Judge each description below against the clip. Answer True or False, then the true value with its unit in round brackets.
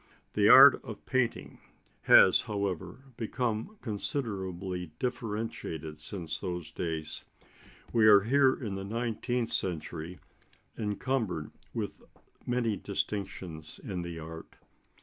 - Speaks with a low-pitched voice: True (100 Hz)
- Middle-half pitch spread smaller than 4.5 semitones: False (5.1 semitones)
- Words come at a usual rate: False (105 wpm)